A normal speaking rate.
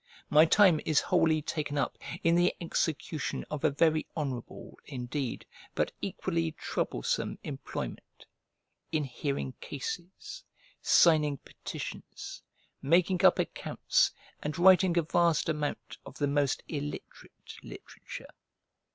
No: slow, 115 wpm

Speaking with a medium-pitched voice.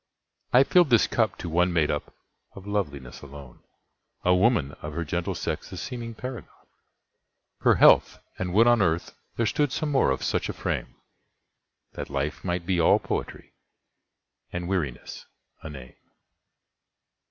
No: very low, 90 Hz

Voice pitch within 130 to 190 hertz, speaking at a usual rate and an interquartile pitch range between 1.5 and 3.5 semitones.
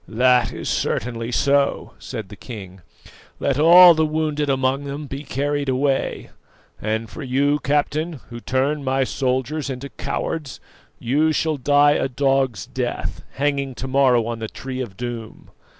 Yes: low, 135 Hz; average, 150 wpm; average, 2.7 semitones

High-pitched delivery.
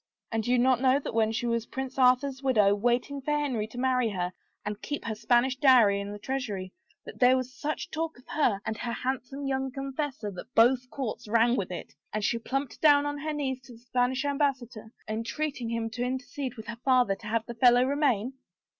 Yes: very high, 250 Hz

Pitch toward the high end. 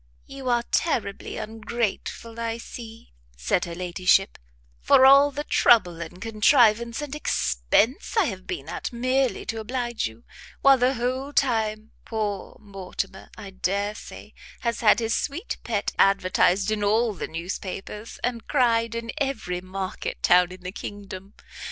Yes: high, 220 Hz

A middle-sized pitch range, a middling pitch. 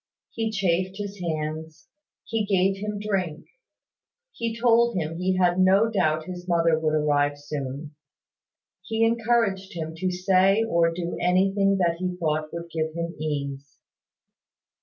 Yes: average, 3.8 semitones; medium, 180 Hz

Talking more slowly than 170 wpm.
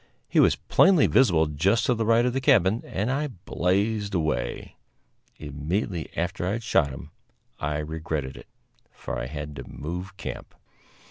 Yes: average, 160 wpm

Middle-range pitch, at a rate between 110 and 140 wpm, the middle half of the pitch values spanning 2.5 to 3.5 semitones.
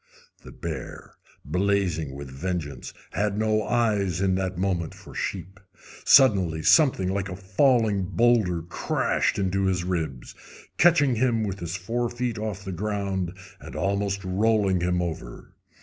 No: very low, 95 Hz; slow, 135 wpm; average, 3.2 semitones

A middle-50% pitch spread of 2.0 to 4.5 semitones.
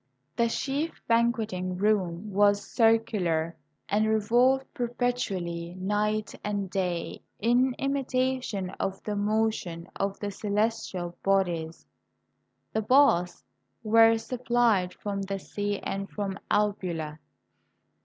Yes: average, 3.6 semitones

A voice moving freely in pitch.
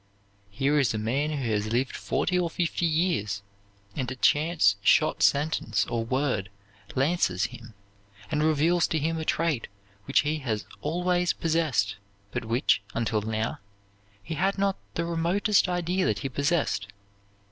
Yes: wide, 6.8 semitones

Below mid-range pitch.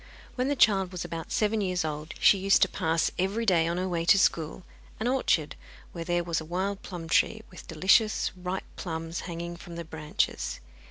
No: medium, 180 Hz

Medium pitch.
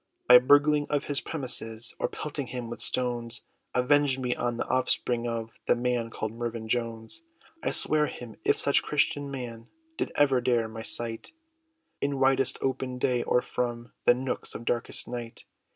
No: low, 125 Hz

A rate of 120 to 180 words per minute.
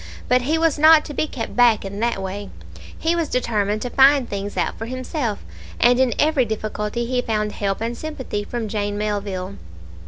No: average, 190 wpm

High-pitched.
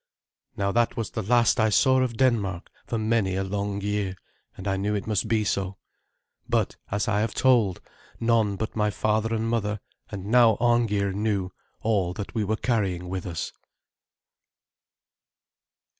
No: low, 105 Hz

